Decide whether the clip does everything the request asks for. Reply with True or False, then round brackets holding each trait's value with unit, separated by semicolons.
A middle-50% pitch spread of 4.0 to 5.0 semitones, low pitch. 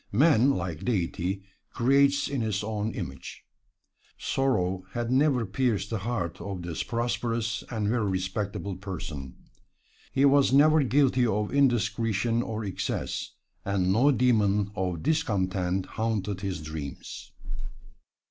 True (4.7 semitones; 105 Hz)